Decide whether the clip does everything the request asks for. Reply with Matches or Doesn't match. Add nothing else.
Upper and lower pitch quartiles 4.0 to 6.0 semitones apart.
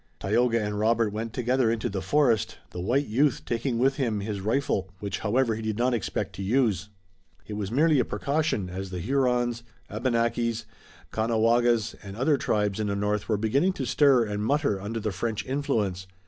Doesn't match